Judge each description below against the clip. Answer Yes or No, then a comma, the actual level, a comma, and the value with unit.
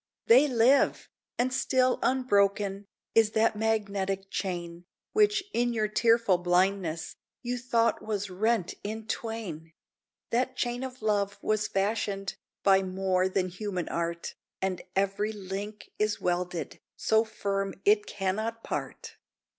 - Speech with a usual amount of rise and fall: Yes, average, 3.2 semitones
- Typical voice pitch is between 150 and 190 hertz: No, high, 205 Hz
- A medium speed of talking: No, slow, 125 wpm